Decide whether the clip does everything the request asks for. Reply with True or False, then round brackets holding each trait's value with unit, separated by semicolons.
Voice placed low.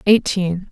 False (190 Hz)